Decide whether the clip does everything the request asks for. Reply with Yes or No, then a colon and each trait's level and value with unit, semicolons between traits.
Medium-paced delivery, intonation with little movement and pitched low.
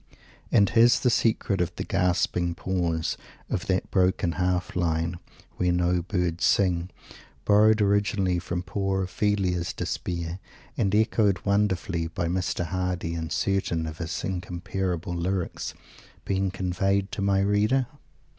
No: slow, 130 wpm; narrow, 2.2 semitones; very low, 90 Hz